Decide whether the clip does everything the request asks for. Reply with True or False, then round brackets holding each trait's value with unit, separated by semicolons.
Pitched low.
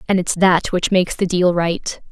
False (180 Hz)